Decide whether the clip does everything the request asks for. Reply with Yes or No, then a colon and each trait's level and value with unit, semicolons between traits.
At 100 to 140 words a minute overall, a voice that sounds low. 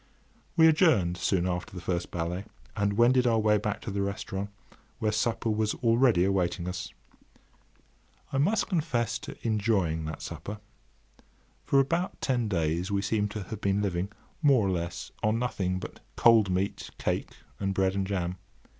No: average, 165 wpm; low, 100 Hz